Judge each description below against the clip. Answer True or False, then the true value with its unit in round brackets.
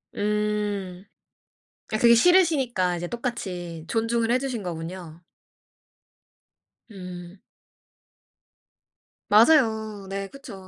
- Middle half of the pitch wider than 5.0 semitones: False (4.4 semitones)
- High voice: True (210 Hz)